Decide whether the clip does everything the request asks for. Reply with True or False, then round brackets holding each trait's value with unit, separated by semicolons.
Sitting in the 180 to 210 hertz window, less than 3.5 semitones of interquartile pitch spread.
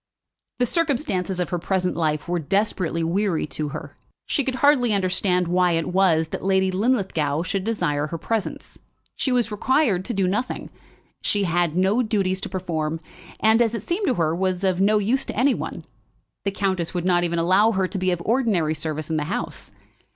False (185 Hz; 4.0 semitones)